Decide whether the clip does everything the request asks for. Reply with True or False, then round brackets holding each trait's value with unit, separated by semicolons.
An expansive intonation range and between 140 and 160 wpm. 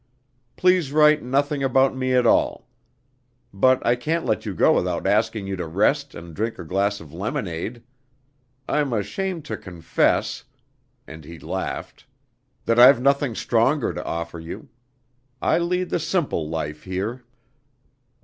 True (7.4 semitones; 145 wpm)